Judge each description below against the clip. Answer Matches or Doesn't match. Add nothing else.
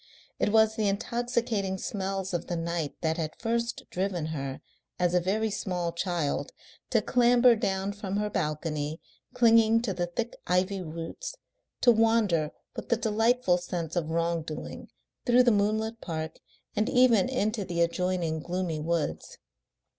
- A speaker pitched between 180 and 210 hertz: Matches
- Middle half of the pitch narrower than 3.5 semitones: Doesn't match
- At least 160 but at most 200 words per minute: Doesn't match